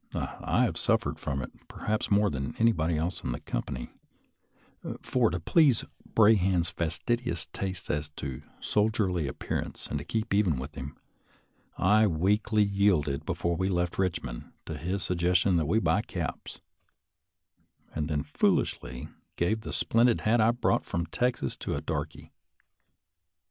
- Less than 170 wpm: Yes, average, 150 wpm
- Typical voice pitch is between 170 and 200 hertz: No, very low, 90 Hz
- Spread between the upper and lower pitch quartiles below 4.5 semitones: No, average, 5.2 semitones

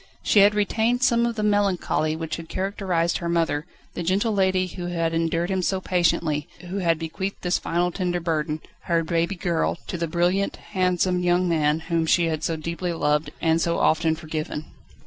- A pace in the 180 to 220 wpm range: Yes, average, 190 wpm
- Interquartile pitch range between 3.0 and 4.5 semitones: No, narrow, 2.4 semitones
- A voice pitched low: No, medium, 175 Hz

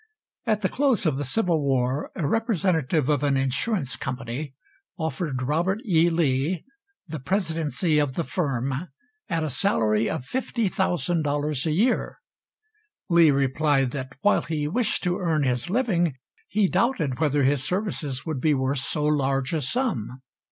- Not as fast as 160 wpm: Yes, average, 150 wpm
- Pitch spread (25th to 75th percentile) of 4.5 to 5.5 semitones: Yes, average, 5.0 semitones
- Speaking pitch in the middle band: Yes, medium, 150 Hz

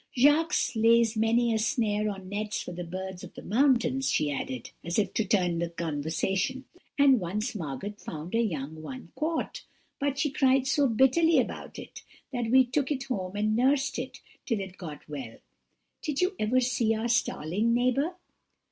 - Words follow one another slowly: No, average, 175 wpm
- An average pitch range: No, wide, 6.1 semitones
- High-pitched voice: Yes, high, 225 Hz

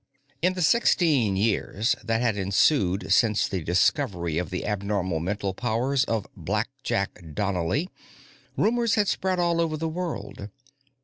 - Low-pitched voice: Yes, low, 110 Hz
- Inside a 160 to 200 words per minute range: No, slow, 135 wpm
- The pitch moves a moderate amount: No, wide, 8.6 semitones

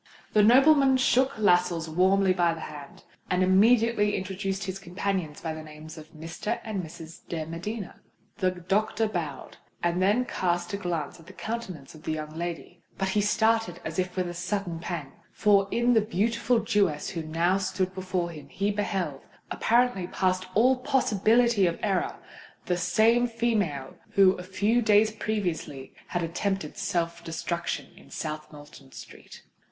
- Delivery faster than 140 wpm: Yes, average, 155 wpm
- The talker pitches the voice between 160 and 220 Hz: Yes, medium, 185 Hz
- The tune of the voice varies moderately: Yes, average, 4.1 semitones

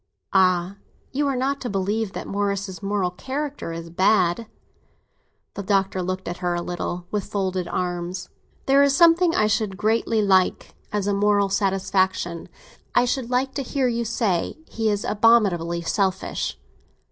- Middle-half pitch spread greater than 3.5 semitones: Yes, average, 3.9 semitones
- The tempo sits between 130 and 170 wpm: Yes, average, 145 wpm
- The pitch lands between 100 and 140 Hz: No, high, 200 Hz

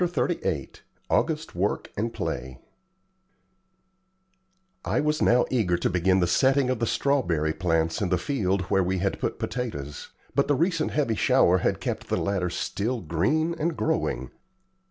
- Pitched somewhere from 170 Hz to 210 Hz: No, low, 100 Hz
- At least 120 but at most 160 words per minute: Yes, average, 155 wpm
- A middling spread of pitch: No, wide, 8.0 semitones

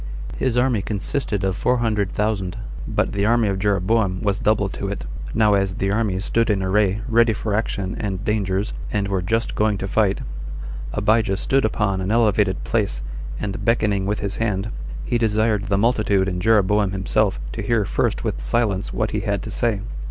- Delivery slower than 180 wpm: No, average, 185 wpm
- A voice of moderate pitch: No, low, 105 Hz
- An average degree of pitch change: No, narrow, 2.2 semitones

